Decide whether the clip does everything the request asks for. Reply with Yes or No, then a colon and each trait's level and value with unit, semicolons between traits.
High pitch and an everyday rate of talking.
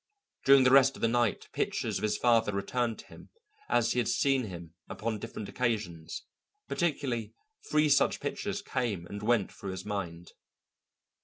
No: low, 115 Hz; average, 165 wpm